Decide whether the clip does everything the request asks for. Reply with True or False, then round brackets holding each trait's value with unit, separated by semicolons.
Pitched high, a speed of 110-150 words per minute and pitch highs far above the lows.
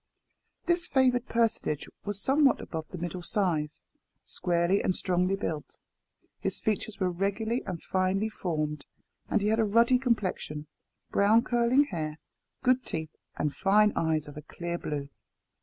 True (195 Hz; 145 wpm; 5.8 semitones)